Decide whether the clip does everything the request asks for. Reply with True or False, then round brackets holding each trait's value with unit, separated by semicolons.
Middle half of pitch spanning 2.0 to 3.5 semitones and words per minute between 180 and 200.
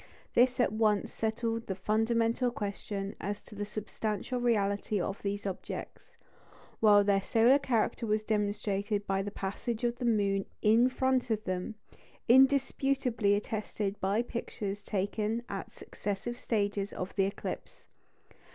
False (2.6 semitones; 135 wpm)